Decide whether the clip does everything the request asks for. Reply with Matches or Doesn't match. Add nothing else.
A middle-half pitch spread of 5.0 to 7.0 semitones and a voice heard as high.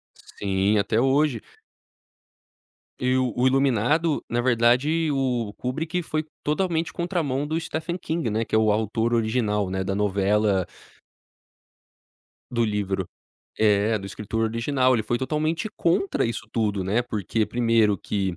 Doesn't match